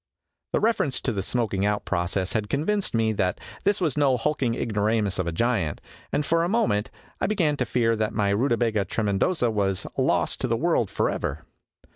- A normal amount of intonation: No, wide, 5.7 semitones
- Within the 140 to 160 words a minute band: No, average, 185 wpm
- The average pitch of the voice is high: No, low, 115 Hz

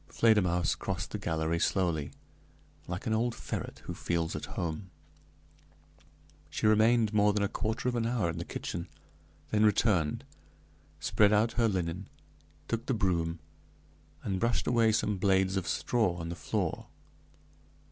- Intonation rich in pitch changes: No, average, 4.2 semitones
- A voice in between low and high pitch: No, low, 100 Hz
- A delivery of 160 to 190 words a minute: No, average, 145 wpm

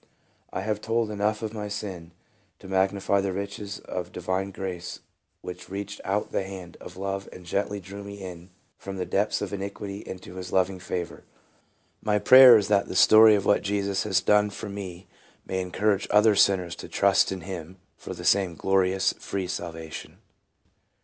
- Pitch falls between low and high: No, very low, 95 Hz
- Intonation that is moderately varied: No, narrow, 1.7 semitones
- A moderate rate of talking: Yes, average, 175 wpm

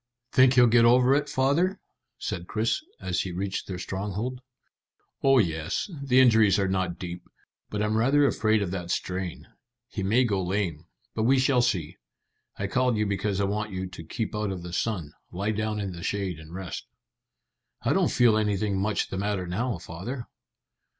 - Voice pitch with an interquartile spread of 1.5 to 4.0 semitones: No, average, 4.5 semitones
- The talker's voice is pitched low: Yes, low, 105 Hz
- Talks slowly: No, average, 185 wpm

